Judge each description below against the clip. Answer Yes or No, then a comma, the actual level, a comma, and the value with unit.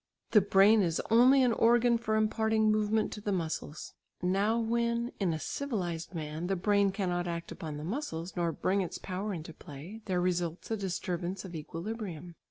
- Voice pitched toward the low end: No, high, 195 Hz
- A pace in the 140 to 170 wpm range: No, average, 180 wpm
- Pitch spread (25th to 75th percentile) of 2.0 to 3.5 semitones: No, average, 4.2 semitones